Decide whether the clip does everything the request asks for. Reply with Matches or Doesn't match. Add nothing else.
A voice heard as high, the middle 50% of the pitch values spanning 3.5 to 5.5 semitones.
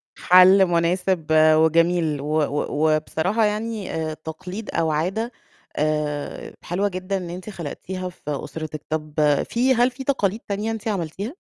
Doesn't match